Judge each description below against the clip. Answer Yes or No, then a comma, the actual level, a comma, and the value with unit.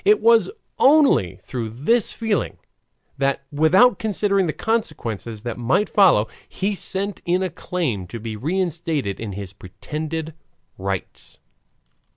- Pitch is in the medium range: Yes, medium, 160 Hz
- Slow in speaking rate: Yes, slow, 130 wpm